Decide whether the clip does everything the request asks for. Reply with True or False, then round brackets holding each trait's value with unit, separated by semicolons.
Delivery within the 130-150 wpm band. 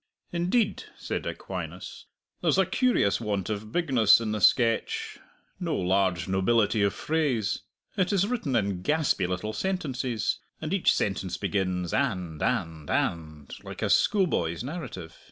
True (135 wpm)